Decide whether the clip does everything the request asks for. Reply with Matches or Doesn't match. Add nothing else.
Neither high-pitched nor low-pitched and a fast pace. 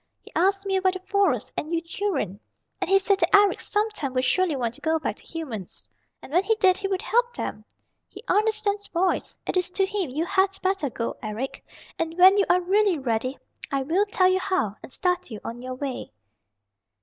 Doesn't match